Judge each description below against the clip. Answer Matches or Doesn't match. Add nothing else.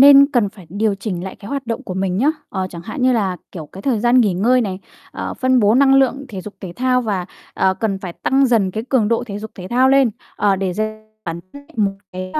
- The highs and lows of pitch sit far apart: Doesn't match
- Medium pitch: Doesn't match